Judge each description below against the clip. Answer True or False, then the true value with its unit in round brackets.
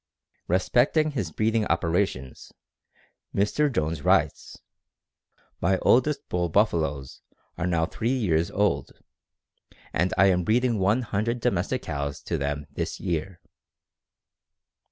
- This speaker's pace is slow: True (115 wpm)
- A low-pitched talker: True (95 Hz)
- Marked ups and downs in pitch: True (5.8 semitones)